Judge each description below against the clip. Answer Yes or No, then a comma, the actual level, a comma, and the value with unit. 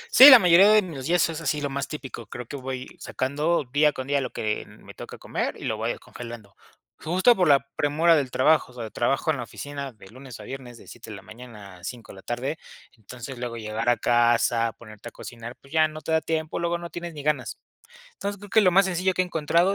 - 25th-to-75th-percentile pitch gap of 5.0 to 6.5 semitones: Yes, wide, 5.5 semitones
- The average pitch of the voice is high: No, medium, 140 Hz